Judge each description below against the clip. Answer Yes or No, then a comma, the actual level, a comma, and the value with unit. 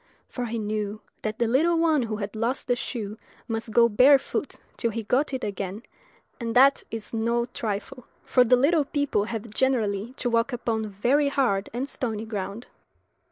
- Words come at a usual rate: Yes, average, 175 wpm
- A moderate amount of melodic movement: Yes, average, 3.3 semitones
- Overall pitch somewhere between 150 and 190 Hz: No, high, 230 Hz